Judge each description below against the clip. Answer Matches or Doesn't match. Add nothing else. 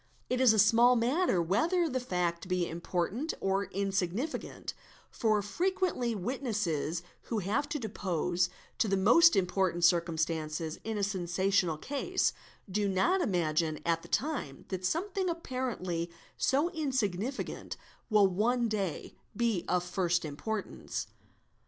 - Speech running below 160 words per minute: Matches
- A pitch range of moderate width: Doesn't match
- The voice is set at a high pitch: Matches